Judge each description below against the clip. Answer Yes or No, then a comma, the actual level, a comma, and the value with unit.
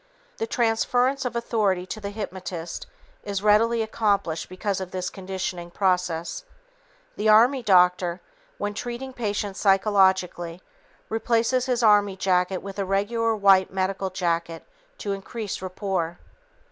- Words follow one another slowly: Yes, slow, 125 wpm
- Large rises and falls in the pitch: No, average, 3.3 semitones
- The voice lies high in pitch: Yes, high, 195 Hz